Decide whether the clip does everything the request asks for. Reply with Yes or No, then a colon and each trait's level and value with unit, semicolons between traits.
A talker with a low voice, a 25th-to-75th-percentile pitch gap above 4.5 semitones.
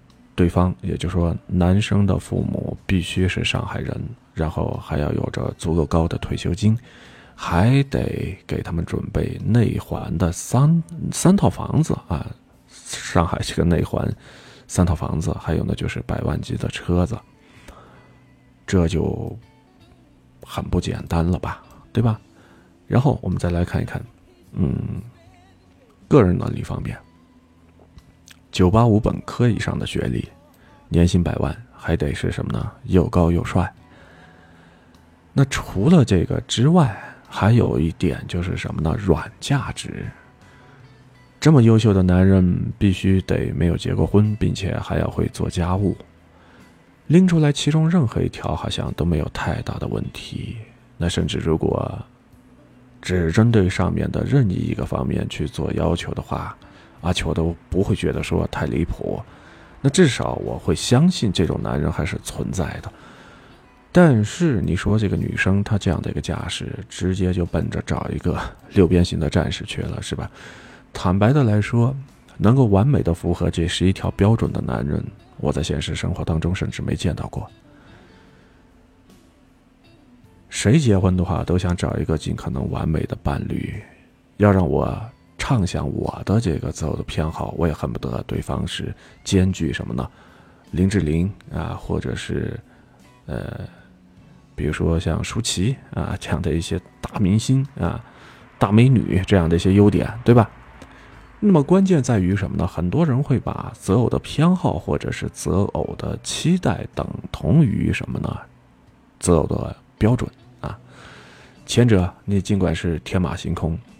Yes: very low, 95 Hz; wide, 5.6 semitones